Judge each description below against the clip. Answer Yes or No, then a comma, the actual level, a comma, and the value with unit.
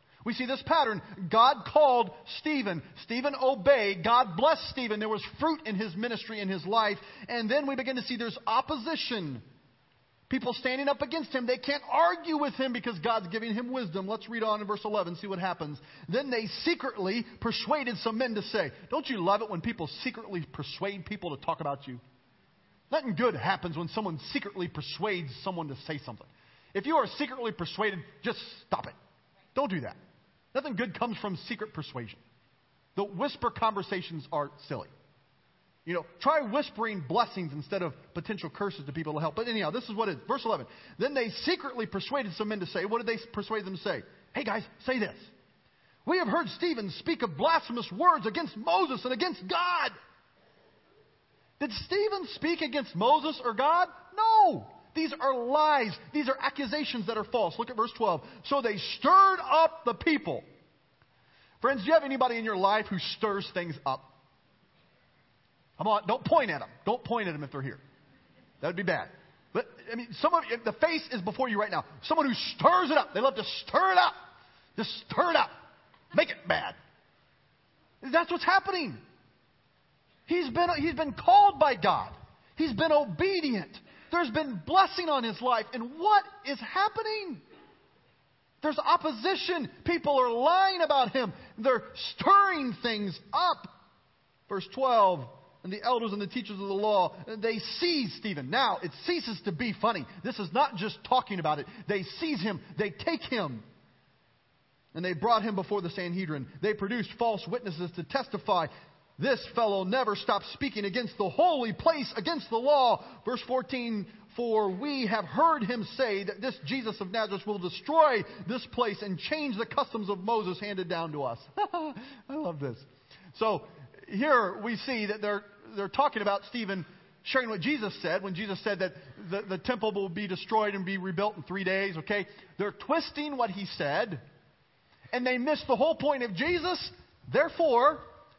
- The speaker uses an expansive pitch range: Yes, wide, 6.5 semitones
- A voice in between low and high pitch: No, high, 225 Hz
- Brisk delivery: No, average, 180 wpm